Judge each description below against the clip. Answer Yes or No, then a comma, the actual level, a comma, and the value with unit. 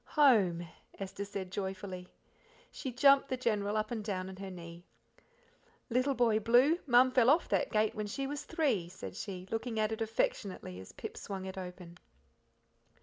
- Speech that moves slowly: No, average, 170 wpm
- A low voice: No, high, 215 Hz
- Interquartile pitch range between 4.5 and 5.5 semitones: Yes, average, 4.8 semitones